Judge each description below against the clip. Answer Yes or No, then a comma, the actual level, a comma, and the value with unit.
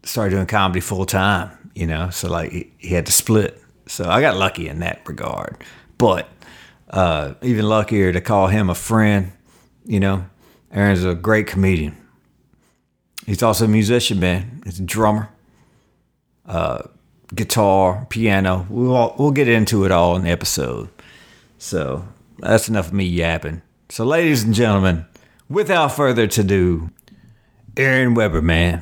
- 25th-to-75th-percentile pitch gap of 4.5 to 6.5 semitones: No, average, 3.7 semitones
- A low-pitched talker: Yes, low, 100 Hz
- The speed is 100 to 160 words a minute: Yes, average, 150 wpm